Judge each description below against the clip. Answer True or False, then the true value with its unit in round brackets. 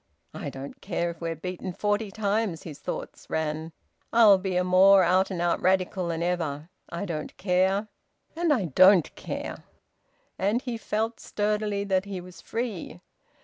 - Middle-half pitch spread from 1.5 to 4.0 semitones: True (3.3 semitones)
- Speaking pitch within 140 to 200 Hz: True (185 Hz)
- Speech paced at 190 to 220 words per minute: False (160 wpm)